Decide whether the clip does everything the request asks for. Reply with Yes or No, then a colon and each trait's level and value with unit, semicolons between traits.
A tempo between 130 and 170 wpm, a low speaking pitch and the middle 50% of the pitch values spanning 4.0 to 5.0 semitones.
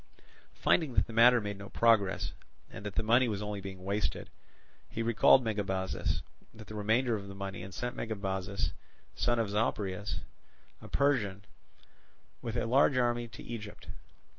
No: average, 160 wpm; low, 105 Hz; average, 3.1 semitones